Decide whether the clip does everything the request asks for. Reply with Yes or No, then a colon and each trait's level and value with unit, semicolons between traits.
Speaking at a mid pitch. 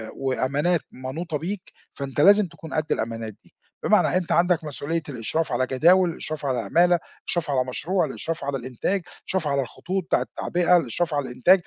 Yes: medium, 155 Hz